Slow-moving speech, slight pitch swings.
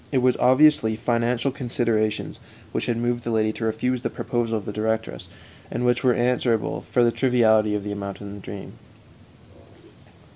No: average, 175 wpm; narrow, 2.3 semitones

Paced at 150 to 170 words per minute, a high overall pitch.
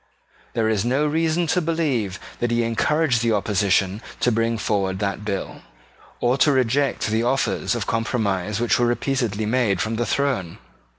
No: average, 165 wpm; low, 115 Hz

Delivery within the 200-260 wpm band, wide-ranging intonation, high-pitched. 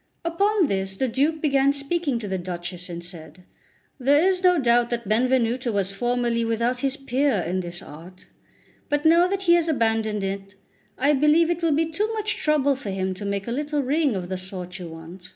Yes: fast, 205 wpm; wide, 7.7 semitones; high, 240 Hz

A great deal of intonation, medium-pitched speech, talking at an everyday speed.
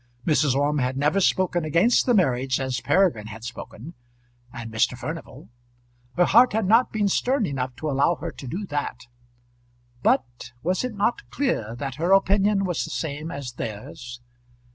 Yes: wide, 7.4 semitones; medium, 150 Hz; average, 165 wpm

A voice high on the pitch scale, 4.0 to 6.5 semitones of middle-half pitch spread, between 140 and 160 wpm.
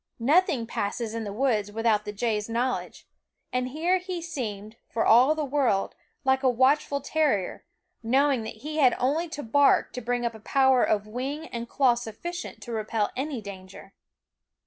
No: high, 245 Hz; average, 4.4 semitones; average, 170 wpm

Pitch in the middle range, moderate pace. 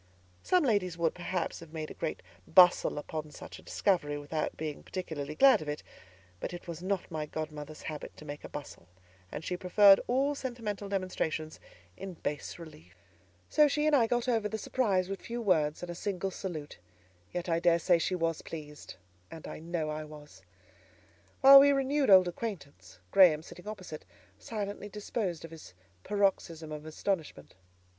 Yes: medium, 175 Hz; average, 170 wpm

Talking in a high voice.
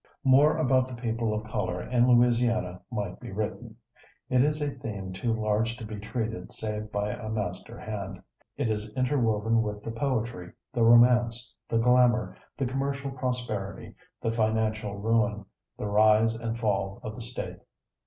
No: low, 115 Hz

